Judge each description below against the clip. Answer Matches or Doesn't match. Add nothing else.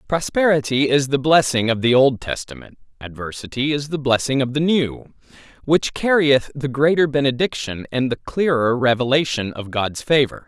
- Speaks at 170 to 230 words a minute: Doesn't match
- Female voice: Doesn't match